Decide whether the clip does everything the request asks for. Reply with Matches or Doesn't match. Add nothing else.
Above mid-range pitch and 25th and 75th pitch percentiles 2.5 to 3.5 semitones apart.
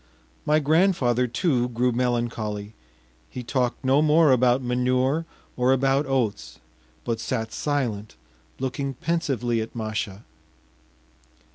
Doesn't match